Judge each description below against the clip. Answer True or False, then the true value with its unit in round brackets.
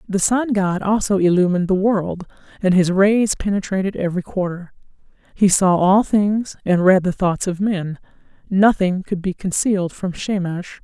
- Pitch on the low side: False (190 Hz)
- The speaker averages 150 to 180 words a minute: True (160 wpm)